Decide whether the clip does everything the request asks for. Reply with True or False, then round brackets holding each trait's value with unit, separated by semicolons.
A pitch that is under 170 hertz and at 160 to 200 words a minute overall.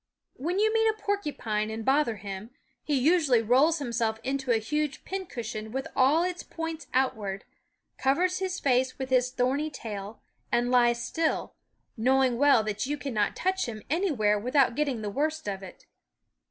False (260 Hz; 165 wpm)